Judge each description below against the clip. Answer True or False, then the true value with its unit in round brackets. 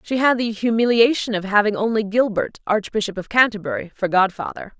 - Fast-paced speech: False (165 wpm)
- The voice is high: True (215 Hz)